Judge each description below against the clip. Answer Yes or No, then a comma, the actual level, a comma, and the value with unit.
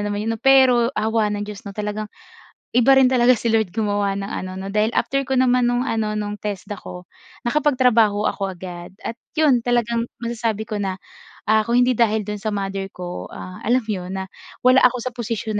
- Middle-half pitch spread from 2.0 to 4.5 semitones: Yes, average, 3.0 semitones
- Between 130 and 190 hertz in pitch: No, high, 220 Hz